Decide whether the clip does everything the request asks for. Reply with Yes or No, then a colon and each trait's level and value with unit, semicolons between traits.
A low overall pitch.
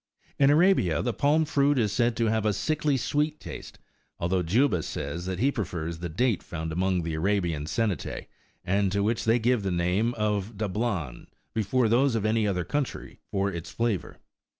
Yes: low, 105 Hz